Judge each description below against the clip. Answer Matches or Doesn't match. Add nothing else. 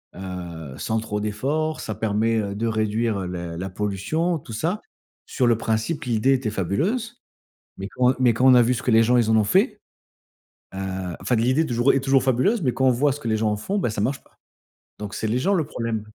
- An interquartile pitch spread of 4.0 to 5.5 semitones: Matches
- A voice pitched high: Doesn't match